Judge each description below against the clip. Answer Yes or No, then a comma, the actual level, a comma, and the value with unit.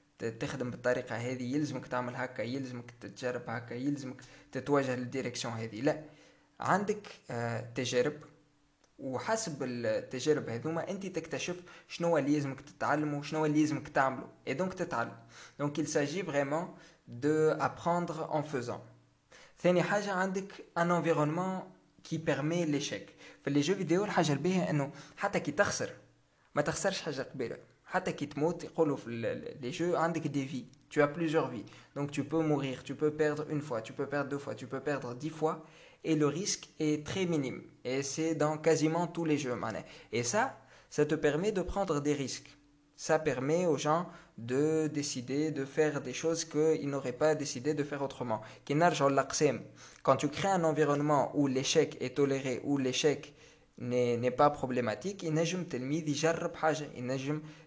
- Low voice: No, medium, 150 Hz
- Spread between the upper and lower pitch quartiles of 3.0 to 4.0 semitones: Yes, average, 3.4 semitones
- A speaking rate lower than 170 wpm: Yes, average, 150 wpm